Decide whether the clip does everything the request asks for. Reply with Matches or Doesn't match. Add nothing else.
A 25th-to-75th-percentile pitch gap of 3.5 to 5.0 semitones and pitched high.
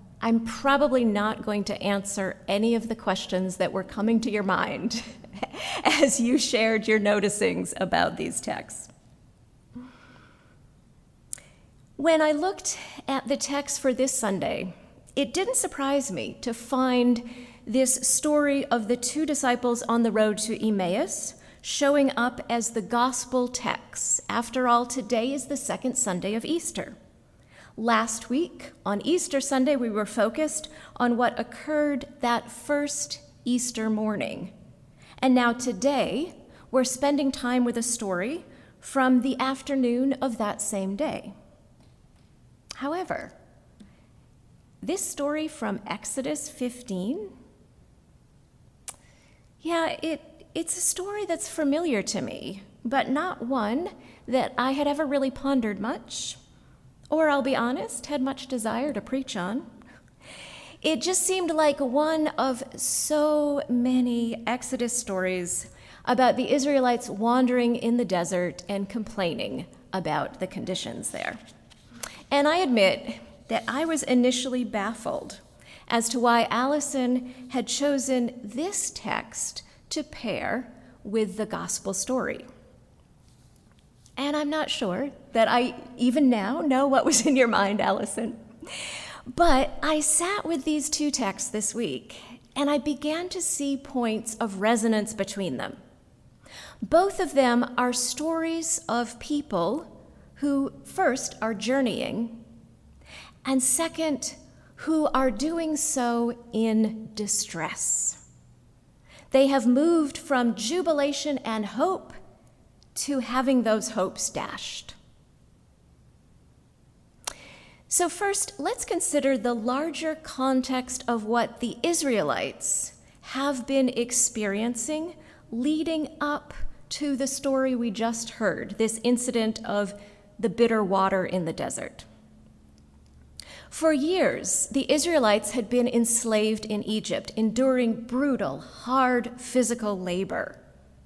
Matches